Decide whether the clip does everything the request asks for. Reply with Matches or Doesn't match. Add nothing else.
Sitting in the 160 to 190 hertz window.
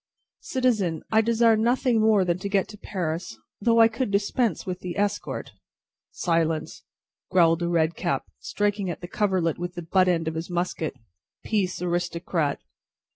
Matches